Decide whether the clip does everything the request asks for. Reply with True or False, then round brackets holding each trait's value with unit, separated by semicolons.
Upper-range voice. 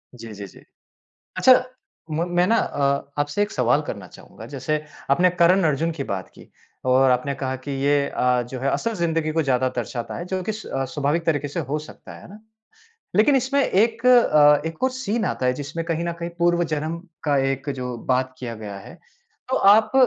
False (150 Hz)